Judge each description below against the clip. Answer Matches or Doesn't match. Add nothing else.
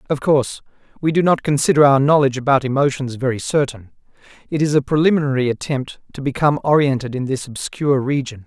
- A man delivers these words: Matches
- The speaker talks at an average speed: Matches